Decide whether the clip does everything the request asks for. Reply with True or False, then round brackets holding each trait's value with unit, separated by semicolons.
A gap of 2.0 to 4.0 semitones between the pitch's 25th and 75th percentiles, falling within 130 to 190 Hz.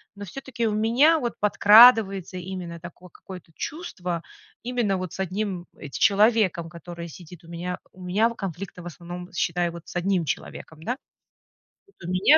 True (3.7 semitones; 185 Hz)